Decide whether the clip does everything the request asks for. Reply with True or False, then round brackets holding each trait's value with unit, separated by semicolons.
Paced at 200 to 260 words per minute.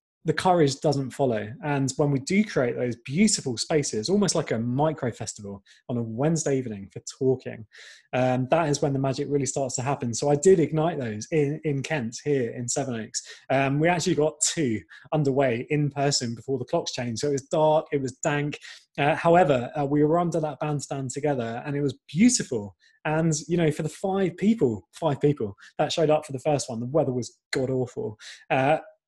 True (205 wpm)